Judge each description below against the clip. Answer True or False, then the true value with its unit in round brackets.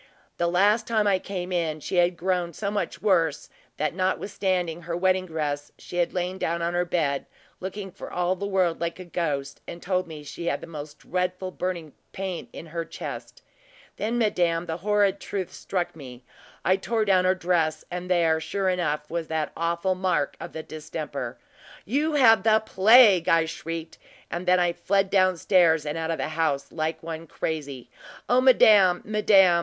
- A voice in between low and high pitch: True (175 Hz)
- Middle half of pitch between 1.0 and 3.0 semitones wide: True (2.7 semitones)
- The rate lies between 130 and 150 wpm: False (185 wpm)